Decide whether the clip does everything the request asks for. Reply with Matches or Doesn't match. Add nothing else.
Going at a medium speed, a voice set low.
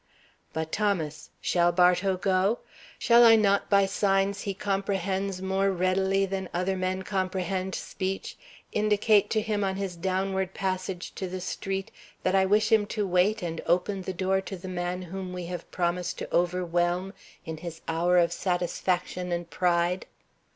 Doesn't match